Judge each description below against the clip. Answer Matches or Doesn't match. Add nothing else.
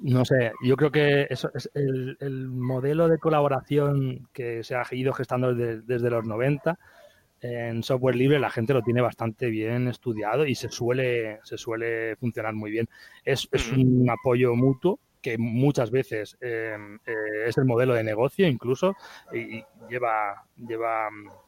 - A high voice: Doesn't match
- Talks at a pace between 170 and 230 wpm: Doesn't match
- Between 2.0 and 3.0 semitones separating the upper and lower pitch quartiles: Matches